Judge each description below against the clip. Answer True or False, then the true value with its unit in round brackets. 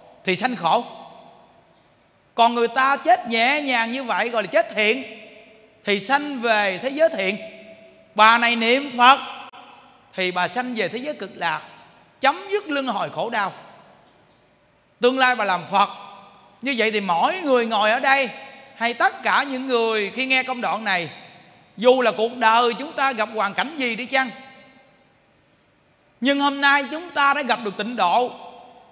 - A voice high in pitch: True (240 Hz)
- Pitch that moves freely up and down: False (3.9 semitones)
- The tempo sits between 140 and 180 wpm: True (175 wpm)